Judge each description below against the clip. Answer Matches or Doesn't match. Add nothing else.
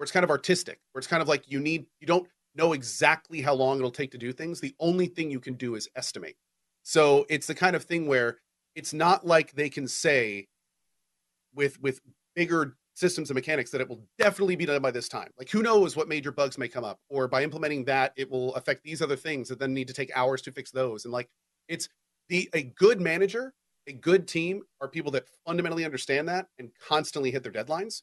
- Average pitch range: Matches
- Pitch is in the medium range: Matches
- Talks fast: Matches